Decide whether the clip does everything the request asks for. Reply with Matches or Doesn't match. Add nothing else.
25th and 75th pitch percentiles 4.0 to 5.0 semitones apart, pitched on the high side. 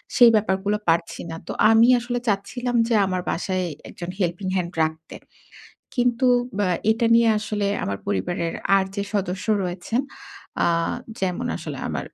Matches